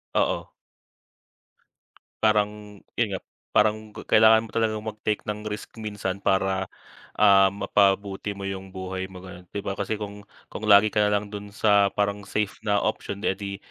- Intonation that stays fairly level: Yes, narrow, 1.4 semitones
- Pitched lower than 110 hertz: Yes, low, 100 Hz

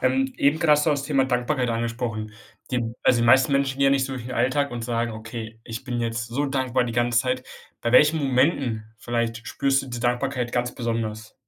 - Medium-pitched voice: No, low, 125 Hz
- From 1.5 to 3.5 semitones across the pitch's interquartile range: Yes, narrow, 2.4 semitones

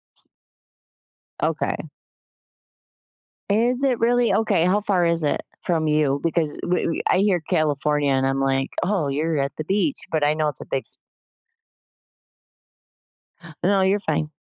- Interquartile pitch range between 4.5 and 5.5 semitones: Yes, average, 5.1 semitones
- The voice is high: No, medium, 165 Hz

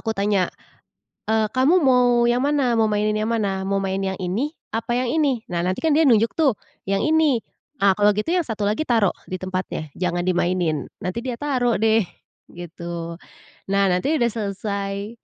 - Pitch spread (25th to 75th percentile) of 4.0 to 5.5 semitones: Yes, average, 4.5 semitones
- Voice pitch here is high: Yes, high, 215 Hz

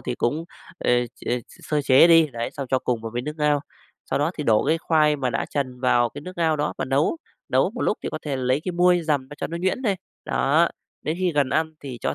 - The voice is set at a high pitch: No, medium, 145 Hz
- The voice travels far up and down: No, average, 3.9 semitones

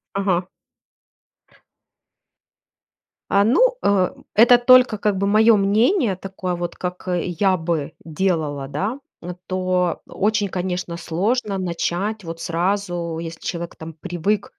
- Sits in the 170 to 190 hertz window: Yes, medium, 185 Hz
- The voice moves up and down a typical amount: Yes, average, 3.2 semitones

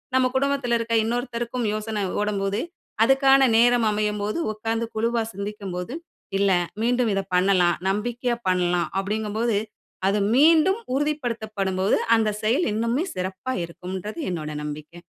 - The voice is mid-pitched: No, high, 215 Hz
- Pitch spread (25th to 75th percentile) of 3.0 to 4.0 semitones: Yes, average, 3.7 semitones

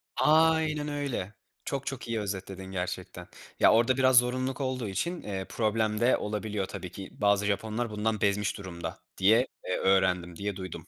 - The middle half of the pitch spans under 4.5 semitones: No, average, 5.1 semitones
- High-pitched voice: No, low, 105 Hz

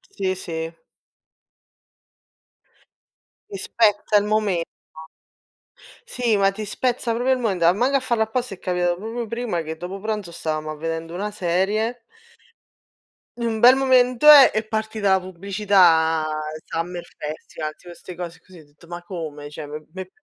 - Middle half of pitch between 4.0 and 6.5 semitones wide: Yes, average, 4.7 semitones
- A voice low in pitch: No, high, 195 Hz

